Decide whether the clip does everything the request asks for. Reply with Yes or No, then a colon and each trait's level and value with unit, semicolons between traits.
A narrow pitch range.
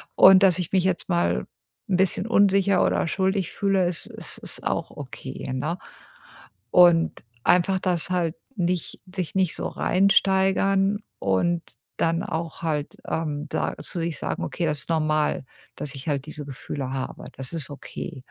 No: average, 4.1 semitones